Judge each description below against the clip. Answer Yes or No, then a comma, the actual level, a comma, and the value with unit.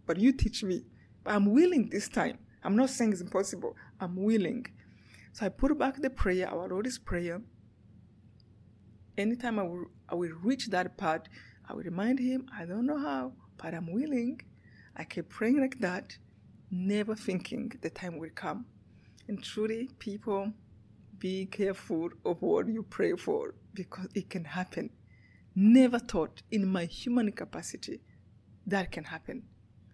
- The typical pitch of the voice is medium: No, high, 195 Hz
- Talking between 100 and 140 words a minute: No, average, 155 wpm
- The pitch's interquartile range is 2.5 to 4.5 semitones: No, wide, 5.4 semitones